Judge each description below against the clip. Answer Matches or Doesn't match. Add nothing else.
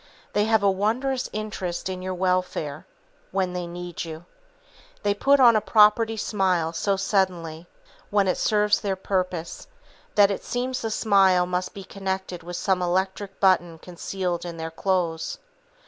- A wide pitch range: Doesn't match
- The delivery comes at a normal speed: Matches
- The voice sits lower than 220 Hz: Matches